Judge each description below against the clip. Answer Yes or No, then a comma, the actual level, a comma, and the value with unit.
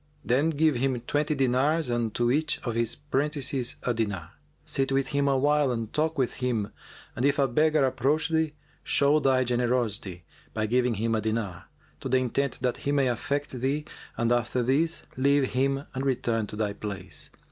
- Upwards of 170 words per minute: Yes, average, 180 wpm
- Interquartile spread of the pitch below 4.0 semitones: Yes, average, 3.2 semitones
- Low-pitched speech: Yes, low, 130 Hz